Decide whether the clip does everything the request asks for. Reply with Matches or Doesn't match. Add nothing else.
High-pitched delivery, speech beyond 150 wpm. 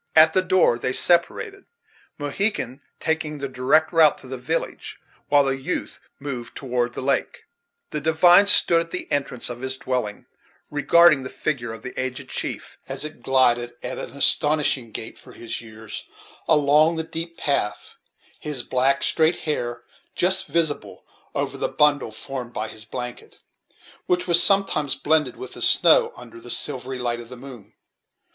Doesn't match